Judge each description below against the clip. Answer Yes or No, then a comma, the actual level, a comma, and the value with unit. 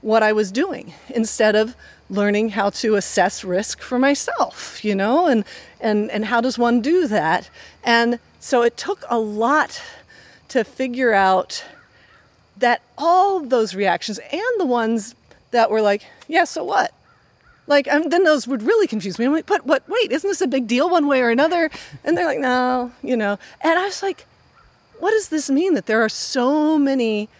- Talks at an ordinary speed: Yes, average, 190 wpm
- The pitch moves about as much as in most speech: No, wide, 6.2 semitones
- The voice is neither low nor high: No, very high, 250 Hz